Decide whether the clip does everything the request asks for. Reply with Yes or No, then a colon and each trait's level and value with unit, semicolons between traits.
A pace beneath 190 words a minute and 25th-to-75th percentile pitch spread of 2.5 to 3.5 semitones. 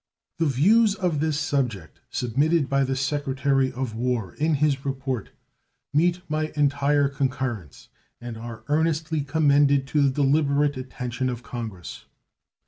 Yes: slow, 135 wpm; average, 2.8 semitones